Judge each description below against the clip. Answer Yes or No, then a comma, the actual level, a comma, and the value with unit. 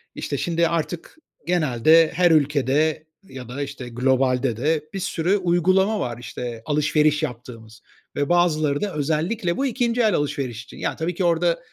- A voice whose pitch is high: No, medium, 155 Hz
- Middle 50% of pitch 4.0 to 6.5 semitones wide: Yes, average, 4.8 semitones